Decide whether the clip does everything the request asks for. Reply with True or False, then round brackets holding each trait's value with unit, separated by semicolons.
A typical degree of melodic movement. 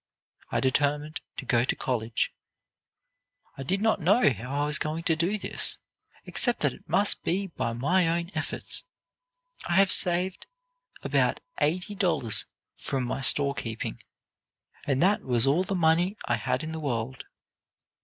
False (5.8 semitones)